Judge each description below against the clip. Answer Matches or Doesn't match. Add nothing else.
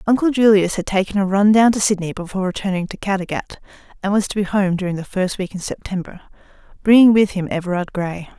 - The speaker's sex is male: Doesn't match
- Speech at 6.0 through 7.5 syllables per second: Matches